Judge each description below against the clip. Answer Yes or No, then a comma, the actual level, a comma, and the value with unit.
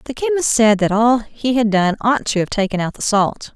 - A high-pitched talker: Yes, high, 225 Hz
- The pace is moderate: No, fast, 255 wpm